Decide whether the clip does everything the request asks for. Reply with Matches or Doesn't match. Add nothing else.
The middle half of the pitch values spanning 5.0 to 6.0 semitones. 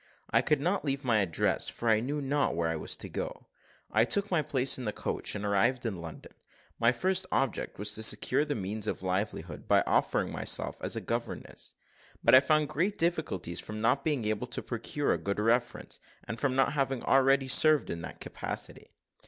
Matches